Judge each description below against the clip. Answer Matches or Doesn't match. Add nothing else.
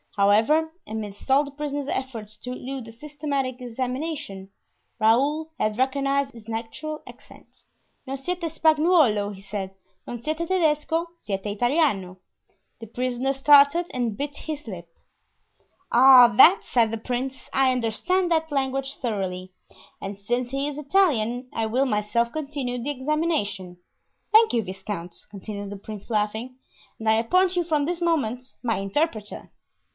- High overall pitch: Matches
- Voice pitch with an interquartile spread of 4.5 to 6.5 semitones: Matches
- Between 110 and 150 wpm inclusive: Matches